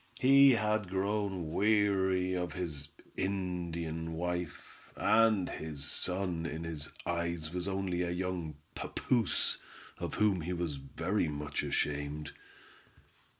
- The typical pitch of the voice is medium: No, very low, 90 Hz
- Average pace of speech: No, slow, 115 wpm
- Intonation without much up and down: No, average, 3.2 semitones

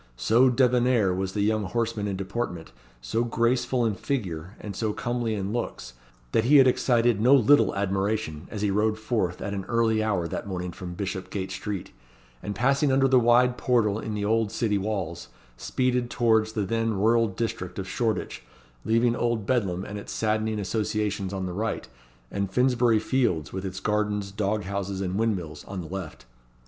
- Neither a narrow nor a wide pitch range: Yes, average, 3.4 semitones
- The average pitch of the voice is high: No, low, 105 Hz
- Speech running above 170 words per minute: Yes, average, 180 wpm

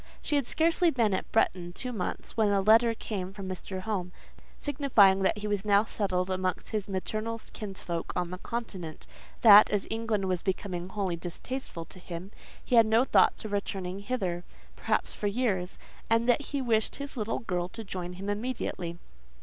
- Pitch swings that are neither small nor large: Yes, average, 3.7 semitones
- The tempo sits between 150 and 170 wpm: No, average, 180 wpm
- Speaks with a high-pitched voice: Yes, high, 205 Hz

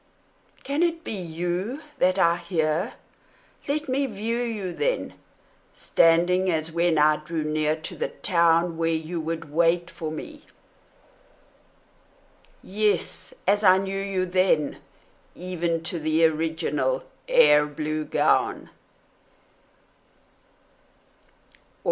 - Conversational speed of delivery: No, slow, 110 wpm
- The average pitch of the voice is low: No, medium, 175 Hz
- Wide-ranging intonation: No, average, 3.7 semitones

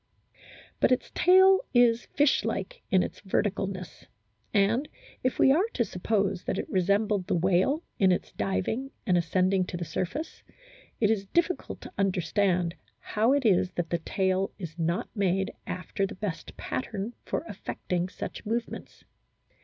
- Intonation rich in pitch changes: No, average, 4.3 semitones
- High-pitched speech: Yes, high, 195 Hz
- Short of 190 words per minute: Yes, average, 155 wpm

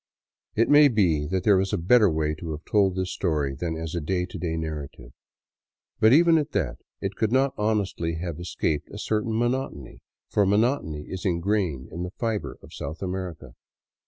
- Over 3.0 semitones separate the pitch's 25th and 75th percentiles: Yes, average, 5.0 semitones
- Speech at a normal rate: Yes, average, 190 wpm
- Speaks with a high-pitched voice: No, very low, 95 Hz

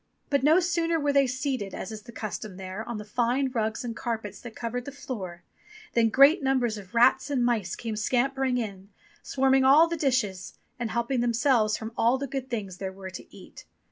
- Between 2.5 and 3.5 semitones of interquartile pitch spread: No, average, 3.9 semitones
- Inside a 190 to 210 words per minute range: Yes, fast, 205 wpm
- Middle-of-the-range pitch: No, high, 240 Hz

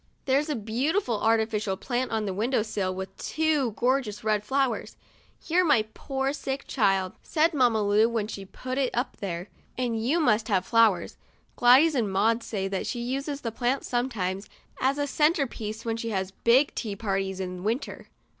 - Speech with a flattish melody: No, average, 4.5 semitones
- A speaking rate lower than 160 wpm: No, average, 185 wpm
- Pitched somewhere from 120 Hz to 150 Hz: No, high, 230 Hz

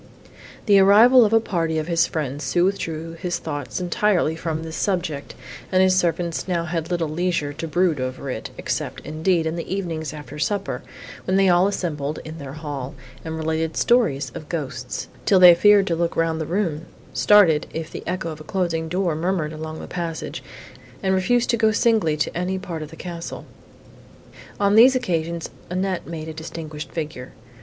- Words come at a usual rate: Yes, average, 185 wpm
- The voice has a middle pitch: Yes, medium, 165 Hz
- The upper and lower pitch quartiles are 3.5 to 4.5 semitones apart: No, average, 3.0 semitones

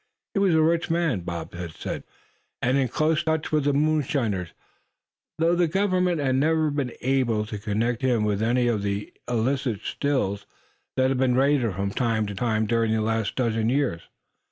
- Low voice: Yes, low, 125 Hz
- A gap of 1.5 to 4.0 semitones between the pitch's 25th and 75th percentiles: No, average, 5.3 semitones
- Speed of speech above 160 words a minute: Yes, average, 180 wpm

